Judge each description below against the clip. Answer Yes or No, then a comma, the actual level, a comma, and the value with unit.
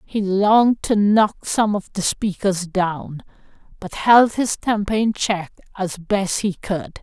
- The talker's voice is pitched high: Yes, high, 200 Hz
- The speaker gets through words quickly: No, average, 160 wpm